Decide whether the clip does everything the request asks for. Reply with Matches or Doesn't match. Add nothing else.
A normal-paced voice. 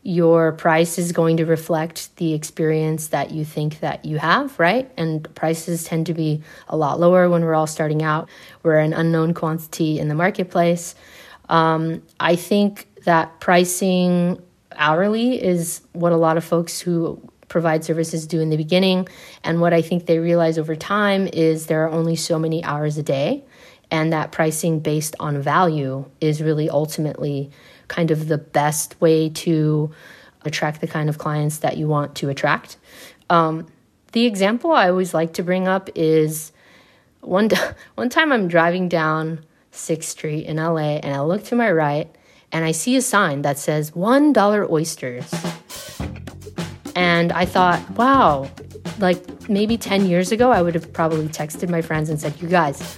Matches